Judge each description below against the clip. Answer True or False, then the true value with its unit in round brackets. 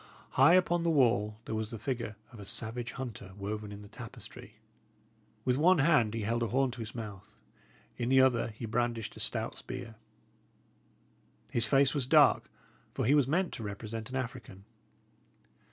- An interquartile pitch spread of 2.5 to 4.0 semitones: True (3.4 semitones)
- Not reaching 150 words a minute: False (175 wpm)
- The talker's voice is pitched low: True (115 Hz)